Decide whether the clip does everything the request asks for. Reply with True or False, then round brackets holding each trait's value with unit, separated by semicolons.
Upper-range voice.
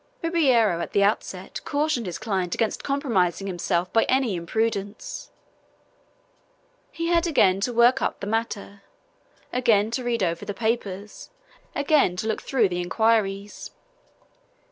True (220 Hz)